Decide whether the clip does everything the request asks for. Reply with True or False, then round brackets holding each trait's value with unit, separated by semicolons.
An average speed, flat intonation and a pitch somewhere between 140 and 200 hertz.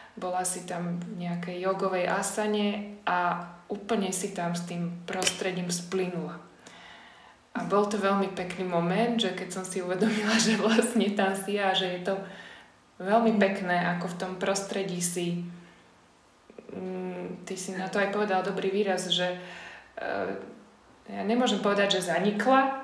True (145 wpm; 2.2 semitones; 190 Hz)